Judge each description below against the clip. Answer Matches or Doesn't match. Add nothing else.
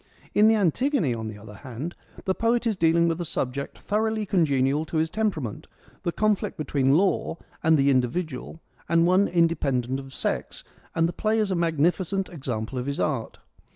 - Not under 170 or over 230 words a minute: Matches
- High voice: Doesn't match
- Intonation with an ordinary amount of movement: Doesn't match